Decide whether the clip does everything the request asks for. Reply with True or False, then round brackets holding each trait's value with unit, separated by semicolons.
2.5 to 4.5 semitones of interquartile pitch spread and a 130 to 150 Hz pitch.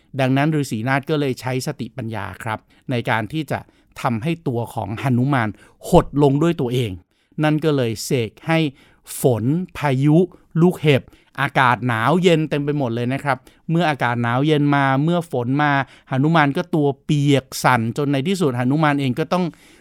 True (3.8 semitones; 140 Hz)